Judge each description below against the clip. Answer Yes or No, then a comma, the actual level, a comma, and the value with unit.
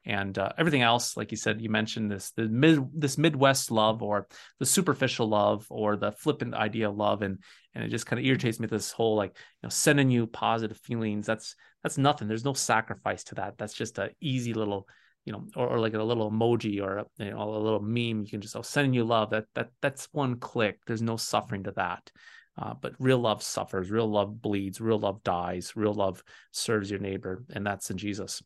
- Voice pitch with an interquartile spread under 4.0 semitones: Yes, narrow, 2.6 semitones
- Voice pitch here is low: Yes, low, 110 Hz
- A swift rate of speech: Yes, fast, 230 wpm